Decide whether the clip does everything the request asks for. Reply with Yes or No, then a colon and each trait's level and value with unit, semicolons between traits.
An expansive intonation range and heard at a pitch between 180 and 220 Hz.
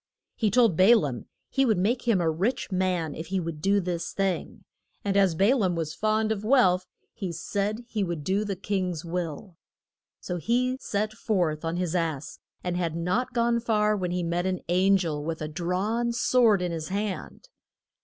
No: average, 4.0 semitones; medium, 185 Hz